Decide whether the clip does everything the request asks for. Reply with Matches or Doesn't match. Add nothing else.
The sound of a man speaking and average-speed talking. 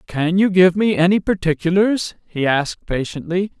Matches